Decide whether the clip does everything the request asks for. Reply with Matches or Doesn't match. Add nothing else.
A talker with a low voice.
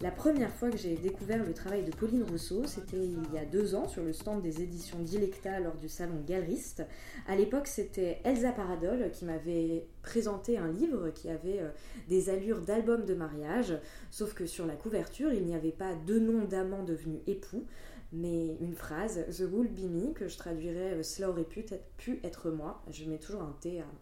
Doesn't match